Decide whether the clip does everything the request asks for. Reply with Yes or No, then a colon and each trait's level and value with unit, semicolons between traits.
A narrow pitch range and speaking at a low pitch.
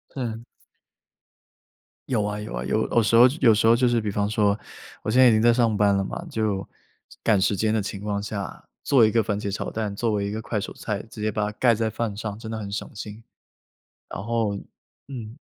Yes: narrow, 2.0 semitones; low, 110 Hz